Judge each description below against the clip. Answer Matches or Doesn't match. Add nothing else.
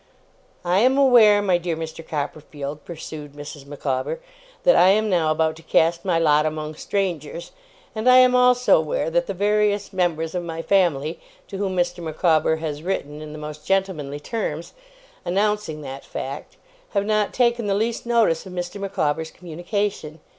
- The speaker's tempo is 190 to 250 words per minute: Doesn't match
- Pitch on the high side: Doesn't match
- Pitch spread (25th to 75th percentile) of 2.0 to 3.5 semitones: Doesn't match